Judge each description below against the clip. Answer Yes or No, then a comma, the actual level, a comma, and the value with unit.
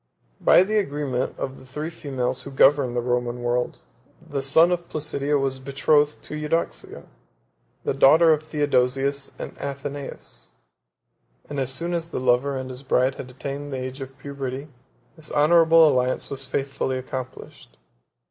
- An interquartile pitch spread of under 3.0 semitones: Yes, narrow, 2.5 semitones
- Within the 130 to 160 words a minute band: Yes, average, 155 wpm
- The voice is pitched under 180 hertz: Yes, medium, 140 Hz